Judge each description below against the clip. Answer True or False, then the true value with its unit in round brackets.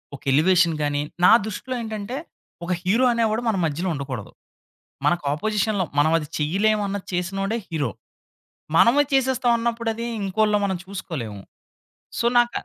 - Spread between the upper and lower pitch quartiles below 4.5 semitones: False (5.5 semitones)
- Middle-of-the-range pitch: False (195 Hz)